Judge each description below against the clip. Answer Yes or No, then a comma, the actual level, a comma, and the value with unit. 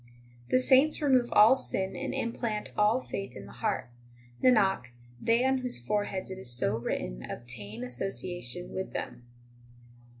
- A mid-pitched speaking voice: No, high, 195 Hz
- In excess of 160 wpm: No, average, 155 wpm